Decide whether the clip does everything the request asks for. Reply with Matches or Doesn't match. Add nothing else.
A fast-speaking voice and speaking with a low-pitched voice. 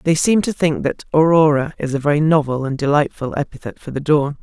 Doesn't match